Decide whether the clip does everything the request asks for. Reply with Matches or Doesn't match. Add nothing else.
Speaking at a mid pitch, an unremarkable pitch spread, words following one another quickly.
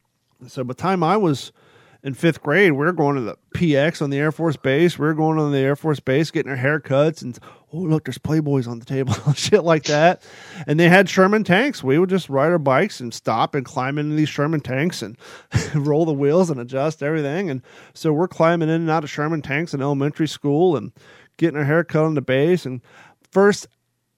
Matches